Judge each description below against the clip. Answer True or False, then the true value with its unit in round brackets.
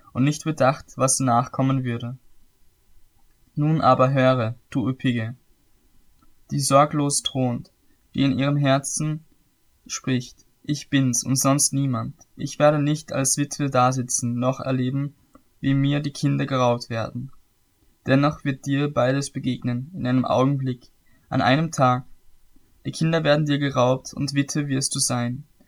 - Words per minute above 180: False (140 wpm)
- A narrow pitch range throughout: True (2.3 semitones)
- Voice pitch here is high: False (135 Hz)